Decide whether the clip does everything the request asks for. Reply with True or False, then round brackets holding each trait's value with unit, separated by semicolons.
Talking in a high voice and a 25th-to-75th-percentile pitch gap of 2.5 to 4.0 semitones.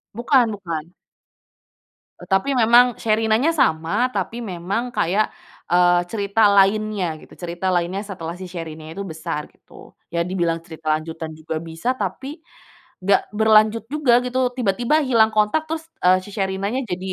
False (195 Hz; 4.6 semitones)